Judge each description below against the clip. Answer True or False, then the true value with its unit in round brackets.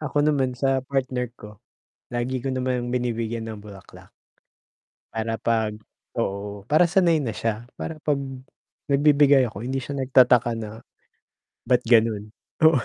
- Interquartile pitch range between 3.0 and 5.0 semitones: True (3.4 semitones)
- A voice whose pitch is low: True (125 Hz)